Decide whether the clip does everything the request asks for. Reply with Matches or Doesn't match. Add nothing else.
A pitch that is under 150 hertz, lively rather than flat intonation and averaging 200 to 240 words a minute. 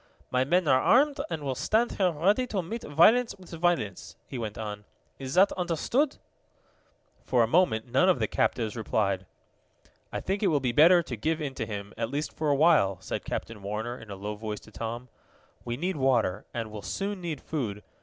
Matches